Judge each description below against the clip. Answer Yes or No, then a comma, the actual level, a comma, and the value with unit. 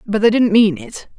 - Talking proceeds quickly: Yes, fast, 255 wpm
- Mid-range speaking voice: No, high, 225 Hz